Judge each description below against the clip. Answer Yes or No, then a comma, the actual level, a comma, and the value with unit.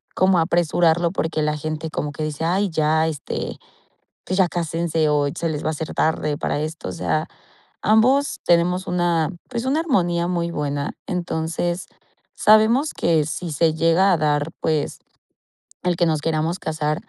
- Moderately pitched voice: Yes, medium, 165 Hz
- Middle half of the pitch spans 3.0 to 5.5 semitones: No, narrow, 2.5 semitones